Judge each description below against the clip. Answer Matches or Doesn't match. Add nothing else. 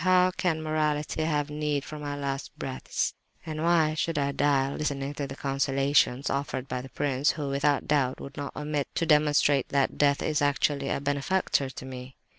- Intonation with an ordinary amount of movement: Doesn't match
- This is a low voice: Doesn't match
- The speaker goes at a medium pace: Matches